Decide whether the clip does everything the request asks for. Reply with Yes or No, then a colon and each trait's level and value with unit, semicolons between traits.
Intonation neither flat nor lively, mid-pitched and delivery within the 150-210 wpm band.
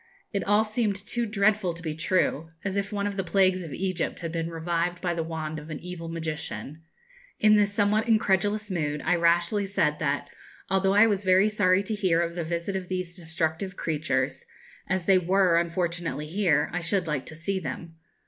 Yes: average, 3.2 semitones; medium, 180 Hz; average, 195 wpm